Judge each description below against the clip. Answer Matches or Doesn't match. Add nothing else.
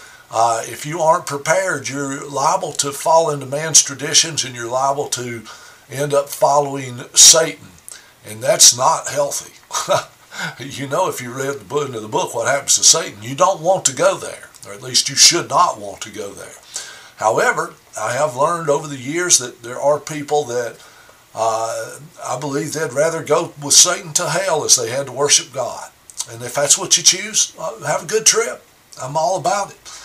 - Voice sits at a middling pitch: Matches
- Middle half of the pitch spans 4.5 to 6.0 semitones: Doesn't match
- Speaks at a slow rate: Doesn't match